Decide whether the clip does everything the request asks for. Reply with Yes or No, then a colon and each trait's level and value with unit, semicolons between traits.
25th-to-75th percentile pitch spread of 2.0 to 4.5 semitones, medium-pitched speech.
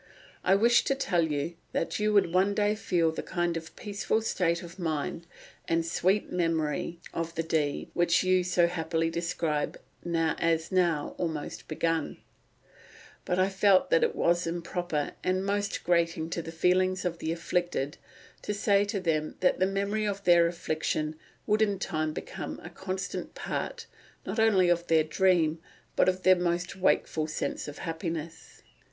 Yes: narrow, 2.4 semitones; medium, 175 Hz